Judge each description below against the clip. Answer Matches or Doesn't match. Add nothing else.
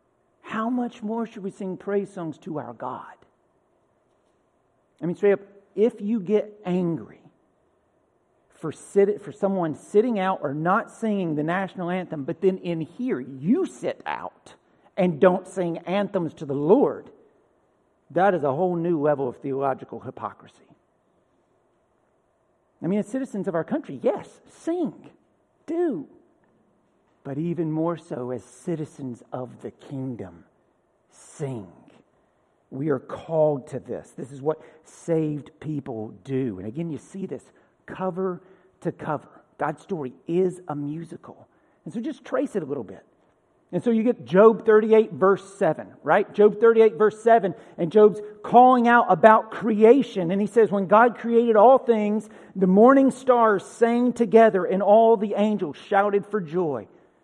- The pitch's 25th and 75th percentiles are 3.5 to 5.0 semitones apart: Doesn't match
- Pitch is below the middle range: Doesn't match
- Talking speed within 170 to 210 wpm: Doesn't match